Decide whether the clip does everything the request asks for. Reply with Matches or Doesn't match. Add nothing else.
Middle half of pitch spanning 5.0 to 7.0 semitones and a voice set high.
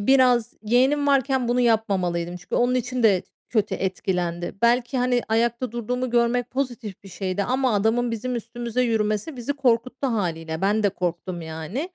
Doesn't match